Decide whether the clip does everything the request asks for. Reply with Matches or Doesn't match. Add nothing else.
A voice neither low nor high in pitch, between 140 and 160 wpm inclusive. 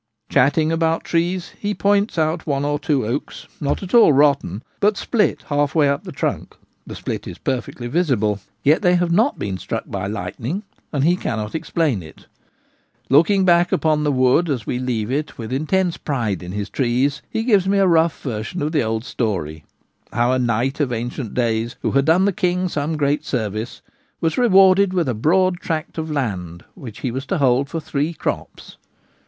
Doesn't match